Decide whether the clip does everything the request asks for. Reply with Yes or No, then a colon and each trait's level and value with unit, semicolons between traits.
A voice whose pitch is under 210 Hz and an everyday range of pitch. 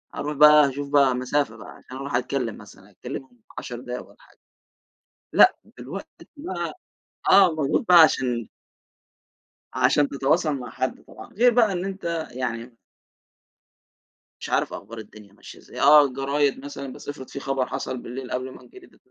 Yes: medium, 140 Hz; average, 3.3 semitones